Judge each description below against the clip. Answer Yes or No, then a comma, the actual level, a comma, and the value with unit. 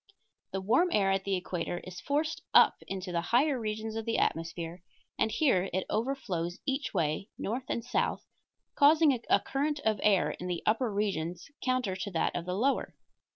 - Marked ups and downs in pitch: Yes, wide, 5.9 semitones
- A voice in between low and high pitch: No, high, 205 Hz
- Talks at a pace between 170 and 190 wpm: Yes, average, 180 wpm